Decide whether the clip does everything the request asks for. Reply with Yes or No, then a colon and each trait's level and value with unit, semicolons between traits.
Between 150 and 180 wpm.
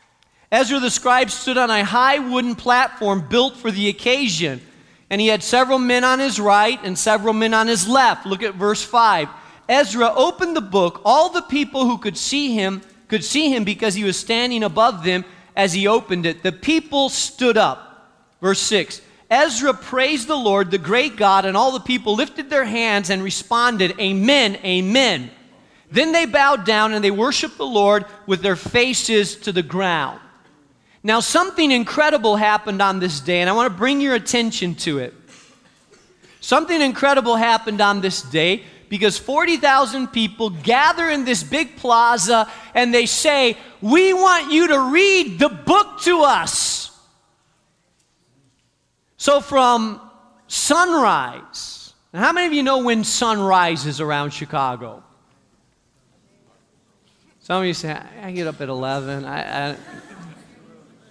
Yes: average, 160 wpm